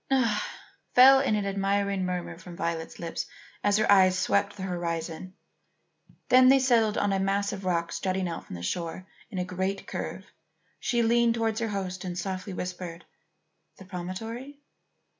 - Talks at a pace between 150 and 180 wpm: Yes, average, 170 wpm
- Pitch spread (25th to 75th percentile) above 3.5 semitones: No, average, 3.2 semitones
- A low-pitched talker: No, high, 195 Hz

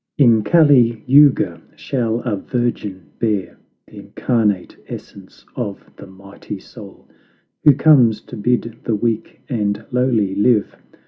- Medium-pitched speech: No, low, 115 Hz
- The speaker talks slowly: Yes, slow, 125 wpm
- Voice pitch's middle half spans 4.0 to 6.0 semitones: No, average, 3.4 semitones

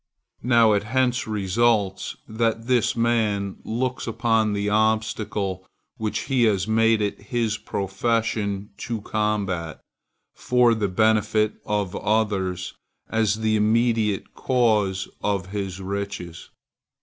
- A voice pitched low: Yes, low, 110 Hz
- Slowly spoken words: Yes, slow, 115 wpm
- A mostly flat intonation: Yes, narrow, 2.3 semitones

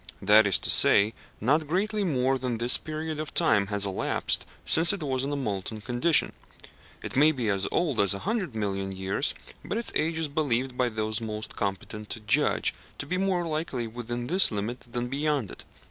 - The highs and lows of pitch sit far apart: Yes, wide, 6.3 semitones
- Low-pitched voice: Yes, low, 125 Hz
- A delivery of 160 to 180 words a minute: No, average, 195 wpm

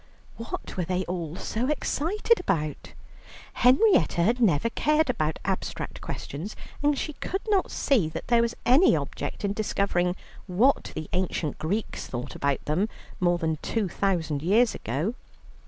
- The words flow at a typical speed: Yes, average, 150 wpm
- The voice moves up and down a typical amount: No, wide, 7.3 semitones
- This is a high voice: Yes, high, 195 Hz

